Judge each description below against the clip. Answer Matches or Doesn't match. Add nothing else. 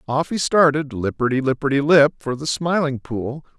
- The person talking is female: Doesn't match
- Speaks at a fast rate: Doesn't match